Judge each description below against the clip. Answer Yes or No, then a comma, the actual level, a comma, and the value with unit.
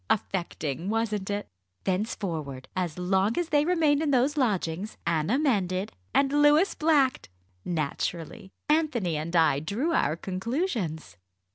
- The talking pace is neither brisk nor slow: No, slow, 125 wpm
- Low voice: No, high, 200 Hz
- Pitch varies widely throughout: Yes, wide, 8.9 semitones